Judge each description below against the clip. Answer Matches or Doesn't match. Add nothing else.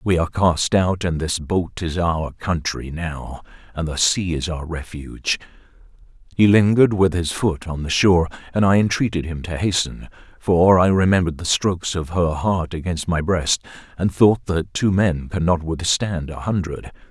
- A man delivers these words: Matches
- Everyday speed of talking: Matches